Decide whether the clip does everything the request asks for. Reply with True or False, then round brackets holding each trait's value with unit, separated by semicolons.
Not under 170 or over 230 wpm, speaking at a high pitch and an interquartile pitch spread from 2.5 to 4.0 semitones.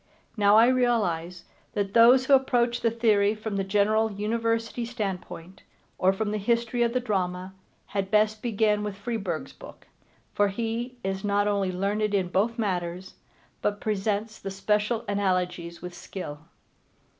False (150 wpm; 210 Hz; 2.9 semitones)